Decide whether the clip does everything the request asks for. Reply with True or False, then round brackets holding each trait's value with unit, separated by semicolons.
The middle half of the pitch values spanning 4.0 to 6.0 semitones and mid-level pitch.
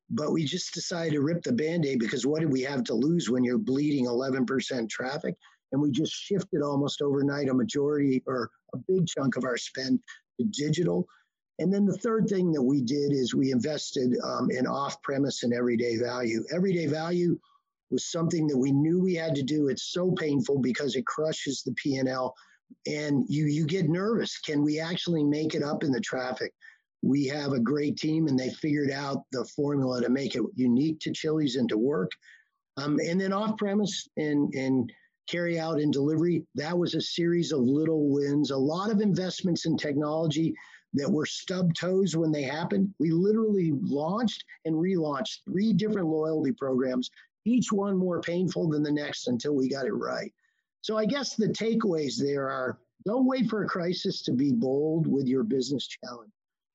True (4.9 semitones; 155 Hz)